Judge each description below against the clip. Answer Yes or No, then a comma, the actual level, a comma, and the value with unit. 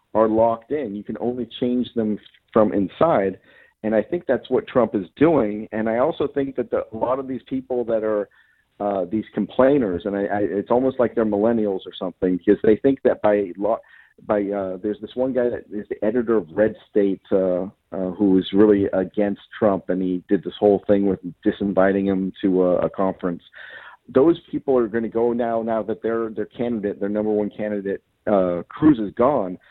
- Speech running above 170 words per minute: Yes, fast, 205 wpm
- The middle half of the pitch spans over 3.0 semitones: No, average, 2.7 semitones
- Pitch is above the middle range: No, low, 105 Hz